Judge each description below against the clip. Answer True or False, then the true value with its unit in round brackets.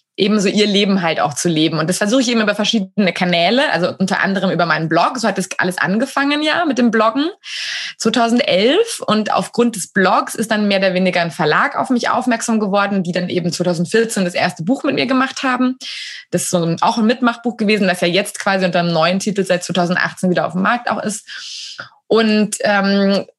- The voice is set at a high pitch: True (205 Hz)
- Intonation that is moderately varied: True (4.5 semitones)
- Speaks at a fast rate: True (210 wpm)